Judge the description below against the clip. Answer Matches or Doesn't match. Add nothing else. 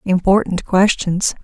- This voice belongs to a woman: Matches